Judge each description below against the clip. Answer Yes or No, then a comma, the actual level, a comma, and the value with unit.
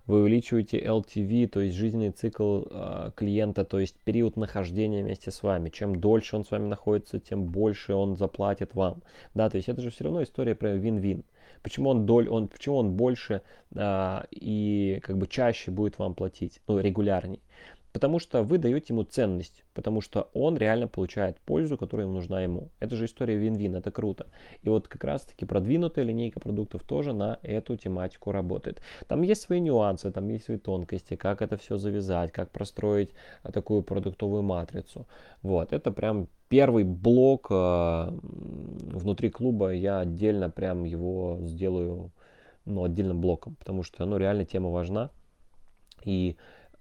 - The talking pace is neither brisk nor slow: No, fast, 165 wpm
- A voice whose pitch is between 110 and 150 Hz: No, low, 100 Hz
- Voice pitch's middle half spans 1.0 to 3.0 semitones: Yes, average, 2.7 semitones